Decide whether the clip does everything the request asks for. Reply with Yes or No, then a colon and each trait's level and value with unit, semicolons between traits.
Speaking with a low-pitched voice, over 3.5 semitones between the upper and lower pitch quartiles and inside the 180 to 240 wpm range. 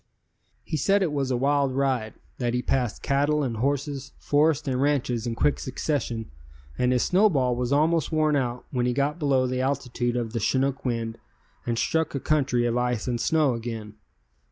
No: low, 130 Hz; average, 3.1 semitones; average, 185 wpm